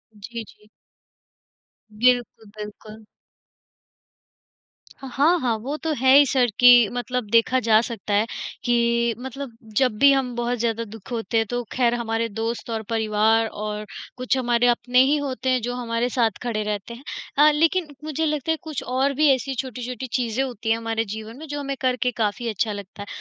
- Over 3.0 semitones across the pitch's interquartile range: No, narrow, 2.6 semitones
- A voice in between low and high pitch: No, high, 240 Hz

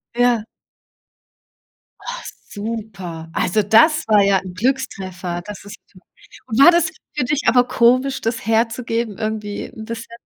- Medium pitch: No, high, 225 Hz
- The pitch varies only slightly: No, average, 3.5 semitones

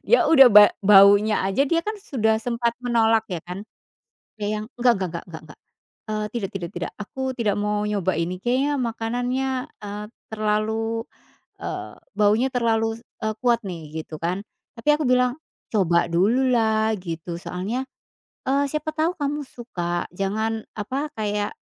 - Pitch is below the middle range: No, high, 220 Hz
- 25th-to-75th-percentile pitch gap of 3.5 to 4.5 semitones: Yes, average, 4.0 semitones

